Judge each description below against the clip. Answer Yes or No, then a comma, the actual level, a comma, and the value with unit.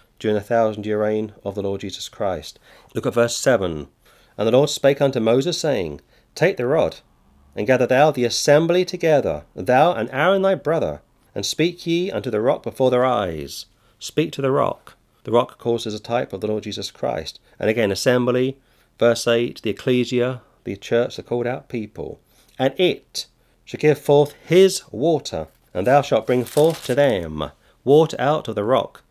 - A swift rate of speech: No, average, 185 wpm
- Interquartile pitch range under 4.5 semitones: No, average, 5.1 semitones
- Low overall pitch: Yes, low, 125 Hz